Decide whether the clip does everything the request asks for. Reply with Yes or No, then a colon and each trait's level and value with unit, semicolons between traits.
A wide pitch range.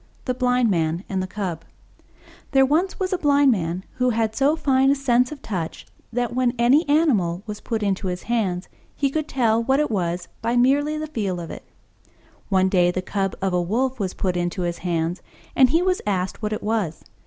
Yes: wide, 6.5 semitones